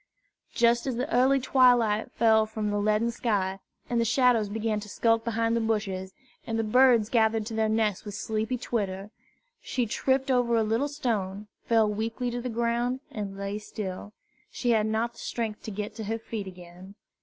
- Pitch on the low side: No, high, 225 Hz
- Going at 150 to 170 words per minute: No, average, 190 wpm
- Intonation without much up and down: Yes, narrow, 2.2 semitones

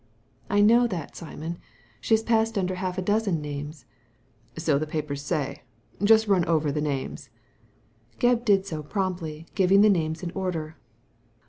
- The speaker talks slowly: No, average, 165 wpm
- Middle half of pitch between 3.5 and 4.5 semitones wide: No, average, 5.0 semitones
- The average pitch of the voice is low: No, medium, 175 Hz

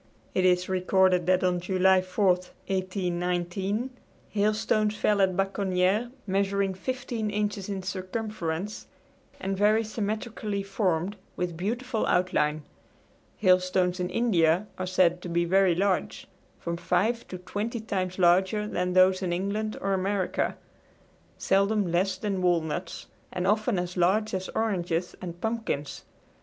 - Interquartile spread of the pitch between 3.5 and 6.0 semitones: No, narrow, 2.5 semitones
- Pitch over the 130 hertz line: Yes, high, 190 Hz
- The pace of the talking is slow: Yes, slow, 130 wpm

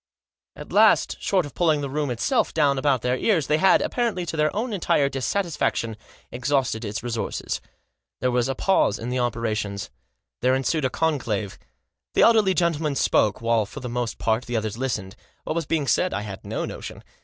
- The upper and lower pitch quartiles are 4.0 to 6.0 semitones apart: Yes, wide, 5.5 semitones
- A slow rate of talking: No, average, 190 wpm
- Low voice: Yes, low, 130 Hz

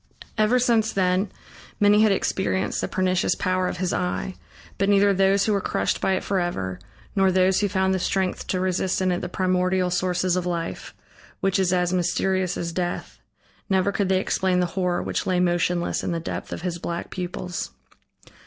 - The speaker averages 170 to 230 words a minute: Yes, average, 190 wpm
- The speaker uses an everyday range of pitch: No, narrow, 1.2 semitones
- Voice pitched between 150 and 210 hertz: Yes, medium, 185 Hz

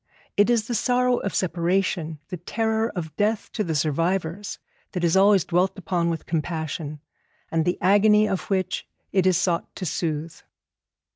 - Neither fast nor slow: Yes, average, 160 wpm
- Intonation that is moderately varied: Yes, average, 3.7 semitones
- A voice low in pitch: No, medium, 185 Hz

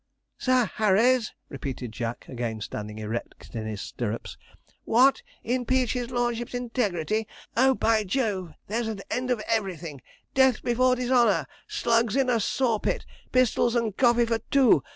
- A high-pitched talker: Yes, high, 230 Hz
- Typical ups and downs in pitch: No, wide, 6.4 semitones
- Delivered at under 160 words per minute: Yes, average, 145 wpm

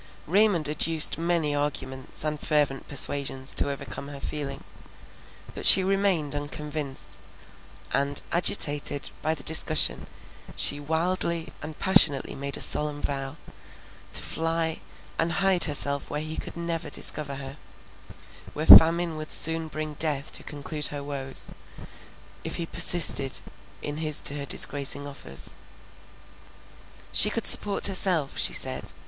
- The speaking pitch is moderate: Yes, medium, 150 Hz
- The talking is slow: Yes, slow, 130 wpm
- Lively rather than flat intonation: No, narrow, 2.6 semitones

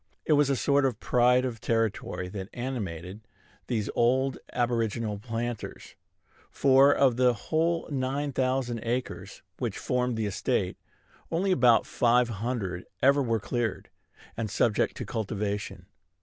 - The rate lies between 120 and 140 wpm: Yes, slow, 135 wpm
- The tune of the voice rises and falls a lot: No, average, 3.4 semitones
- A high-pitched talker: No, low, 120 Hz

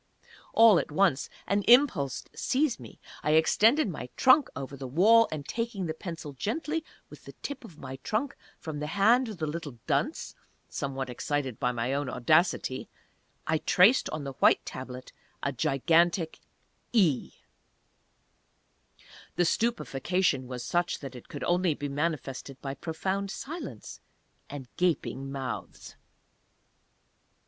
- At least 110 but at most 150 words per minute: Yes, average, 140 wpm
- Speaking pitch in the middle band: Yes, medium, 160 Hz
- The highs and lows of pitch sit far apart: Yes, wide, 6.7 semitones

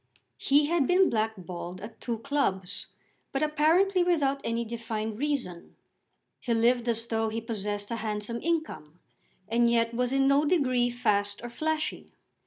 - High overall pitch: Yes, high, 235 Hz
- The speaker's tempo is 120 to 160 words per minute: Yes, average, 150 wpm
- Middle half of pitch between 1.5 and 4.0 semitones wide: No, average, 4.7 semitones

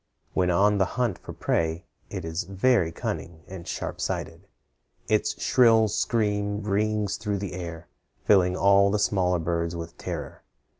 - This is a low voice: Yes, low, 100 Hz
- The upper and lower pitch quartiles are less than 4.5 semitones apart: Yes, average, 3.4 semitones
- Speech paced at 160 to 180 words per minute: No, average, 150 wpm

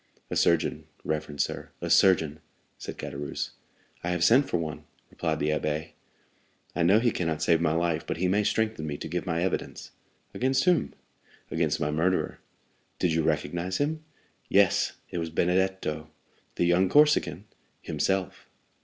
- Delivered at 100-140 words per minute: No, average, 155 wpm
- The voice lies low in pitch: Yes, very low, 85 Hz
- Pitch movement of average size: Yes, average, 3.4 semitones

